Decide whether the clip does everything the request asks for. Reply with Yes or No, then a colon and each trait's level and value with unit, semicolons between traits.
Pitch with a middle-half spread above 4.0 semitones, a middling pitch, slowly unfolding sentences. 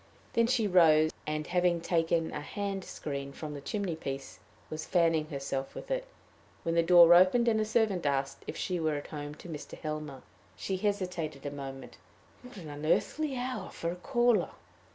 No: average, 5.0 semitones; medium, 165 Hz; average, 180 wpm